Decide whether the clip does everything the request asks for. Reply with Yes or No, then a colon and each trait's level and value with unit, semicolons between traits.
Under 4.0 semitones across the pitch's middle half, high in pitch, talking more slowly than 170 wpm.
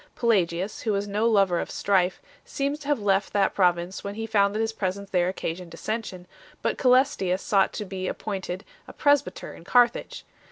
No: average, 3.3 semitones; high, 200 Hz; average, 195 wpm